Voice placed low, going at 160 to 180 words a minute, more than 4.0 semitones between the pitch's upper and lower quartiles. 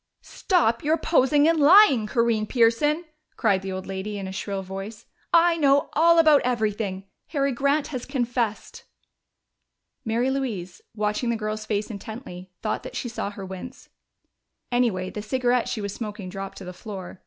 No: high, 225 Hz; average, 165 wpm; average, 5.3 semitones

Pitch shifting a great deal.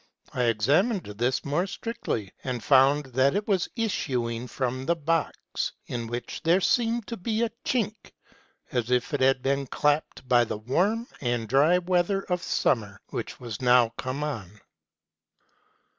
Yes: wide, 6.8 semitones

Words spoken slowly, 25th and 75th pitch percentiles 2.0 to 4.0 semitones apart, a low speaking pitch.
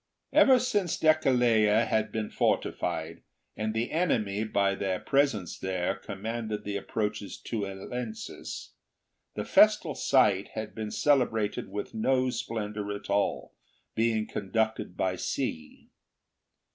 Yes: slow, 120 wpm; average, 2.7 semitones; low, 110 Hz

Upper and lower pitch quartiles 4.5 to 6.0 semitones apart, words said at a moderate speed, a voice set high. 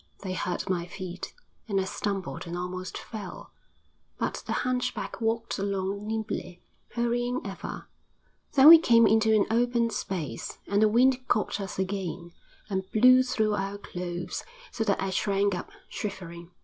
No: average, 3.7 semitones; average, 150 wpm; high, 200 Hz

